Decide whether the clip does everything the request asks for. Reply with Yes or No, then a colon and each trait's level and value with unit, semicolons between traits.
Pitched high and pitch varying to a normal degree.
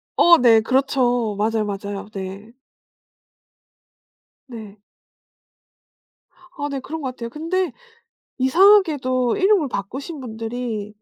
Yes: very high, 250 Hz; average, 5.0 semitones